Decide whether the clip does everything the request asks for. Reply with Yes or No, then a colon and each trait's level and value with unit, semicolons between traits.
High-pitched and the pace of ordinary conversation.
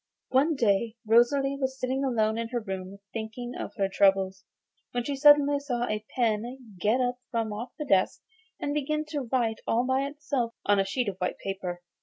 Yes: high, 240 Hz; average, 190 wpm